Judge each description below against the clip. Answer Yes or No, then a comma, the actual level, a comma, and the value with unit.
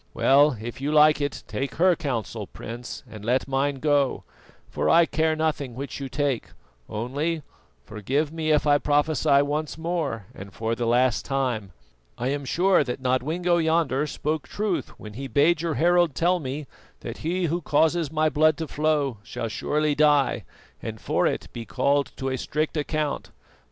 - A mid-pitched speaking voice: Yes, medium, 145 Hz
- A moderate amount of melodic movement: Yes, average, 3.3 semitones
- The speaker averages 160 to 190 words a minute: Yes, average, 170 wpm